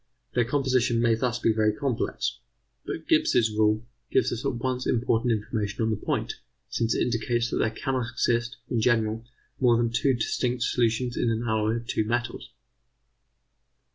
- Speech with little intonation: Yes, narrow, 1.7 semitones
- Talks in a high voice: No, low, 120 Hz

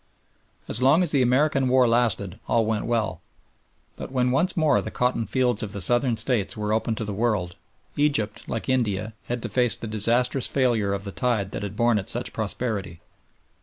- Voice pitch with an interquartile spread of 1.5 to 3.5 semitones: Yes, average, 3.2 semitones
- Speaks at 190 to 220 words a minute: Yes, average, 195 wpm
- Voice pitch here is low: Yes, low, 115 Hz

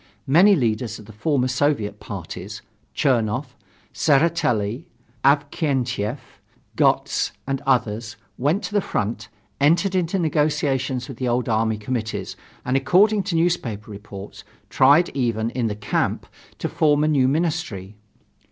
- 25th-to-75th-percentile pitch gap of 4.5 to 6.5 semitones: Yes, wide, 5.6 semitones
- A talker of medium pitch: No, low, 130 Hz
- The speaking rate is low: Yes, slow, 130 wpm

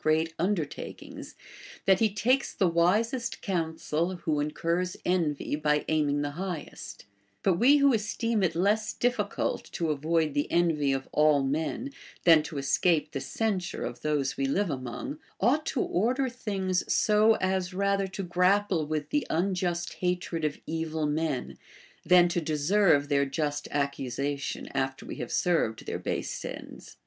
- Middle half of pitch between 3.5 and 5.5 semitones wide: Yes, average, 5.0 semitones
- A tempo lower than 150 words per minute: No, average, 155 wpm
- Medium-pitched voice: Yes, medium, 170 Hz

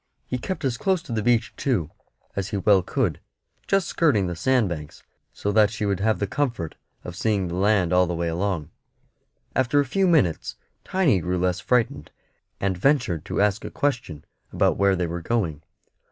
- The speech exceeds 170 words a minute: Yes, average, 190 wpm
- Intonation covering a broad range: Yes, wide, 6.0 semitones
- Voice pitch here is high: No, low, 100 Hz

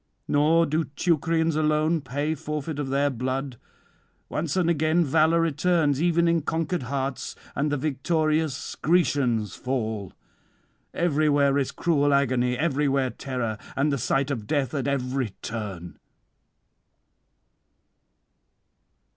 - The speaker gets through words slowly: Yes, slow, 115 wpm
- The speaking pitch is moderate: Yes, medium, 145 Hz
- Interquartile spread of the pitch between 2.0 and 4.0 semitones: Yes, average, 3.3 semitones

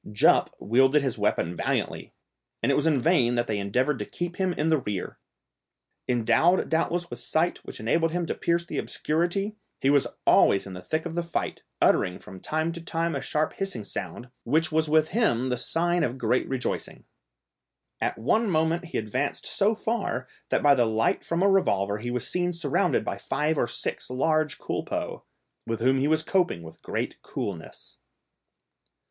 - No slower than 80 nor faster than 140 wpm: No, average, 185 wpm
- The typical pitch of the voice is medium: Yes, medium, 150 Hz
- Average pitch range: No, wide, 5.9 semitones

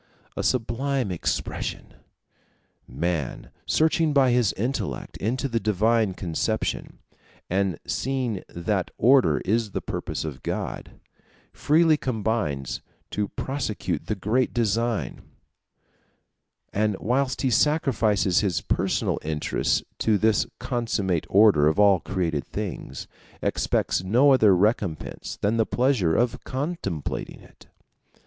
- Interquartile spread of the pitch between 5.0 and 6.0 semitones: Yes, wide, 5.4 semitones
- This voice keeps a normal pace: No, slow, 110 wpm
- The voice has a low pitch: Yes, low, 110 Hz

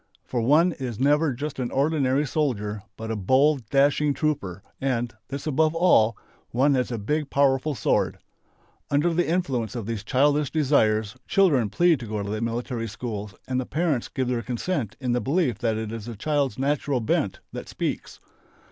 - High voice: No, low, 130 Hz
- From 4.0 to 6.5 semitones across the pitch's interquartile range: Yes, average, 4.5 semitones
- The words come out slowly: No, average, 180 wpm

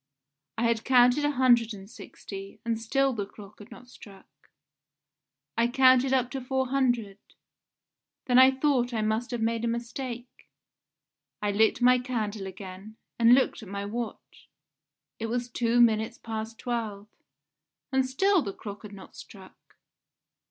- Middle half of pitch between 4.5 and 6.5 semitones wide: No, average, 2.9 semitones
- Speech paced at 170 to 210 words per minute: No, average, 150 wpm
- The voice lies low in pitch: No, high, 235 Hz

